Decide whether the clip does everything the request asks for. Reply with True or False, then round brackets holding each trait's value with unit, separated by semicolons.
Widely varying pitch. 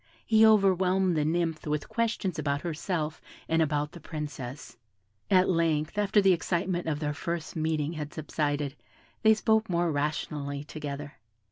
False (3.8 semitones)